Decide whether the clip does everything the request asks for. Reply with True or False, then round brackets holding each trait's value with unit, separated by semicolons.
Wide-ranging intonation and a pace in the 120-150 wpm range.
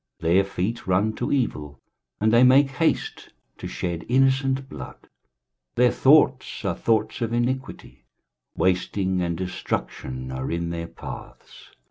True (7.1 semitones; 135 wpm)